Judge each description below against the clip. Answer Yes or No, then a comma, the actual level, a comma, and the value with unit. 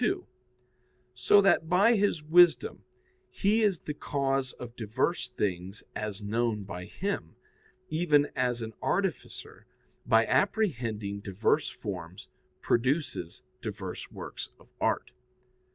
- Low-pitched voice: Yes, low, 125 Hz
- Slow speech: Yes, slow, 115 wpm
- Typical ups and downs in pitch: No, wide, 8.6 semitones